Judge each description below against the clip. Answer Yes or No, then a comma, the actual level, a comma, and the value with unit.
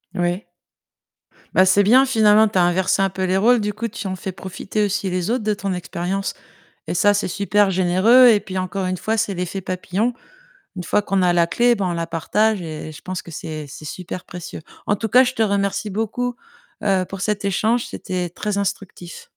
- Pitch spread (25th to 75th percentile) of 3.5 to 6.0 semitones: No, average, 2.7 semitones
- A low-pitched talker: No, high, 195 Hz